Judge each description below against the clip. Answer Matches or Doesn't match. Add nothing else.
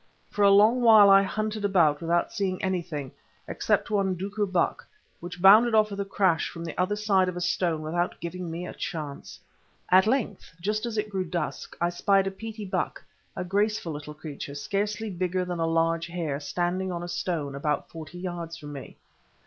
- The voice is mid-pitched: Matches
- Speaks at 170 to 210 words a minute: Matches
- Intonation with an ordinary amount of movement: Matches